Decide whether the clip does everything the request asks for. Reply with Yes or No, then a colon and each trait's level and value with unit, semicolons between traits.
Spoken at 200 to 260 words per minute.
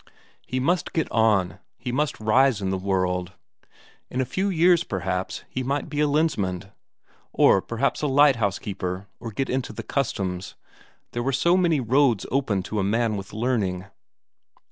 No: average, 165 wpm